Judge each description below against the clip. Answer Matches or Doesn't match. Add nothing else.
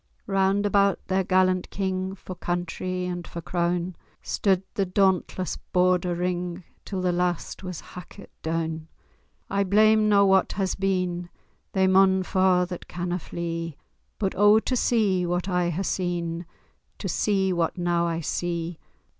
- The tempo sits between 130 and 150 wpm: Matches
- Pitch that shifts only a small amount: Matches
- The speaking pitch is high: Doesn't match